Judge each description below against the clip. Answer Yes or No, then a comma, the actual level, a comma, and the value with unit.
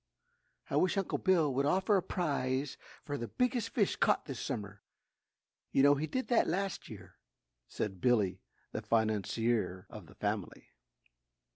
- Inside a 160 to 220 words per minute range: No, average, 150 wpm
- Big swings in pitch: Yes, wide, 8.6 semitones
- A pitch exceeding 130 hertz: Yes, medium, 140 Hz